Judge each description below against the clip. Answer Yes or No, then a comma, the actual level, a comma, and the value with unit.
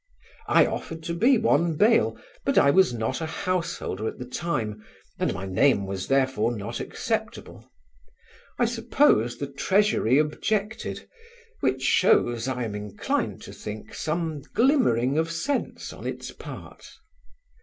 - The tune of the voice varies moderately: No, wide, 7.1 semitones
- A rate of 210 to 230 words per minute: No, average, 140 wpm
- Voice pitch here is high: No, medium, 140 Hz